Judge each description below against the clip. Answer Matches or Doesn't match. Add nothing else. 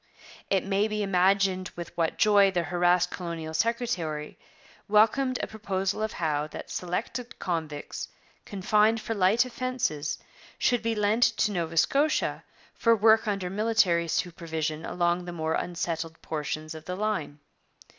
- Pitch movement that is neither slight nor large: Matches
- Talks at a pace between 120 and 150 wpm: Matches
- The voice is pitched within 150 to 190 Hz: Matches